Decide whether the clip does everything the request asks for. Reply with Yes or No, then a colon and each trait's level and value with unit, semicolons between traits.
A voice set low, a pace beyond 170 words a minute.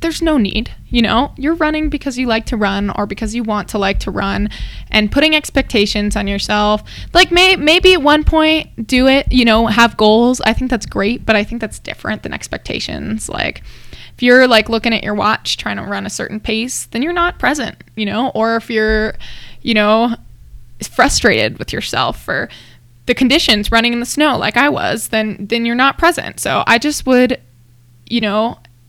No: high, 230 Hz; average, 200 wpm